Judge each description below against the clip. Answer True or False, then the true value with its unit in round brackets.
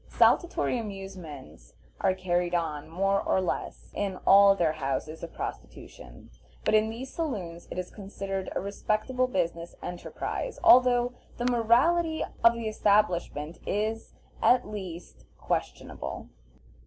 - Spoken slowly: True (125 wpm)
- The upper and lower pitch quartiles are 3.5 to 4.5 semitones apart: False (5.1 semitones)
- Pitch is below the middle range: False (195 Hz)